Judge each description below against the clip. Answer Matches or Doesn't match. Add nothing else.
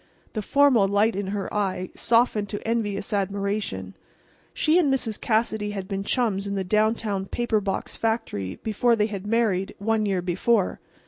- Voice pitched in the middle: Doesn't match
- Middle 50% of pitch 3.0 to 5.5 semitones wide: Doesn't match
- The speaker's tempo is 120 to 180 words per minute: Matches